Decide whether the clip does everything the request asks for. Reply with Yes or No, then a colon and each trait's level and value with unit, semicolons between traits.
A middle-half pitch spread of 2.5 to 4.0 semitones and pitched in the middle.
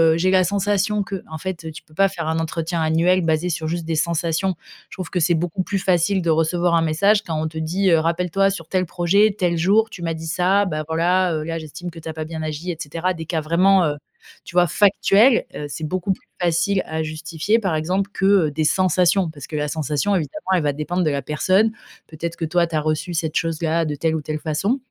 Yes: average, 2.8 semitones; medium, 170 Hz